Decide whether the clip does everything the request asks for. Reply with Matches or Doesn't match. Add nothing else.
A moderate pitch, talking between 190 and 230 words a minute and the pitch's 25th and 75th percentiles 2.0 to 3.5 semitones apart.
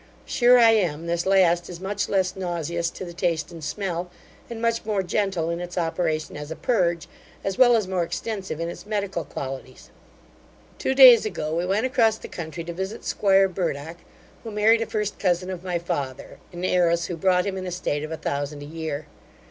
Matches